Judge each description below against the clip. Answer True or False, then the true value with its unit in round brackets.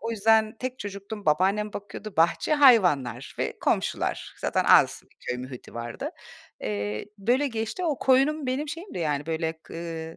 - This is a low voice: False (200 Hz)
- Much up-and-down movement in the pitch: True (8.0 semitones)